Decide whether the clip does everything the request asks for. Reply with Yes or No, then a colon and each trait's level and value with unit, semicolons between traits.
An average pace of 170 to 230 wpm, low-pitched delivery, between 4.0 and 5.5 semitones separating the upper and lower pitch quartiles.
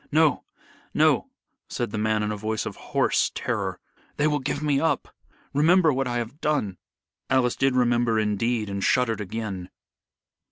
No: average, 160 wpm; low, 120 Hz; average, 4.8 semitones